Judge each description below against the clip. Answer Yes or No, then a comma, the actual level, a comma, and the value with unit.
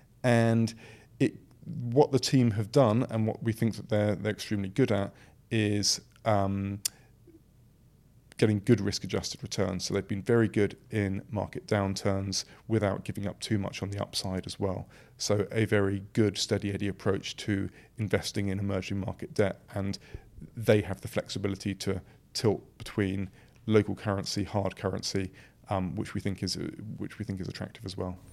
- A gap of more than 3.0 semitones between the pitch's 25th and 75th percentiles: No, average, 2.7 semitones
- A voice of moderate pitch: No, low, 105 Hz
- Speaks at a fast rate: No, average, 165 wpm